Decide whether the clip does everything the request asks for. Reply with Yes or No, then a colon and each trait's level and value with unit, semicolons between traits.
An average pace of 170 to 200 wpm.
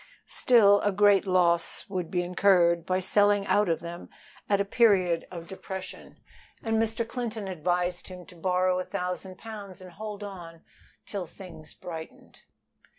No: average, 150 wpm